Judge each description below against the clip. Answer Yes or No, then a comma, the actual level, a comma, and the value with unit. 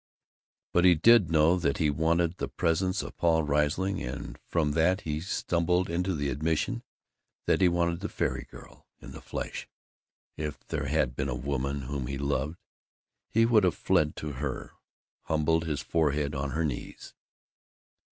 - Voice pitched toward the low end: Yes, very low, 80 Hz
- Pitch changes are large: No, average, 3.4 semitones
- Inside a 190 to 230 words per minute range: No, average, 165 wpm